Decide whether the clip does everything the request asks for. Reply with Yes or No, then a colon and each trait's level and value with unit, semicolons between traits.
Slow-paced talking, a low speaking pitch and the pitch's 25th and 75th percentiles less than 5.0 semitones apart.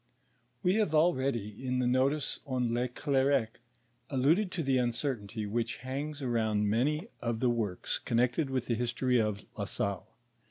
No: average, 155 wpm; low, 125 Hz; average, 3.2 semitones